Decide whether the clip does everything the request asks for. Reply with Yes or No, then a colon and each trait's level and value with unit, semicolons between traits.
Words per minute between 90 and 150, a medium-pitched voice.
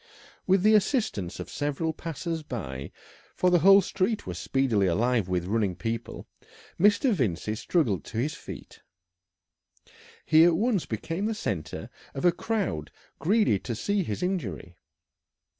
Yes: average, 140 wpm; medium, 145 Hz